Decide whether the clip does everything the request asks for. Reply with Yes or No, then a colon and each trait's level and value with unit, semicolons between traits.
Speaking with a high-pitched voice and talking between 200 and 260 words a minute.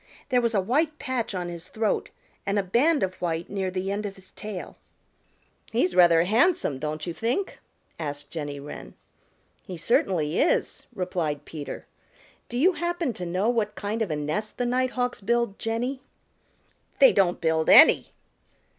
No: high, 195 Hz; average, 165 wpm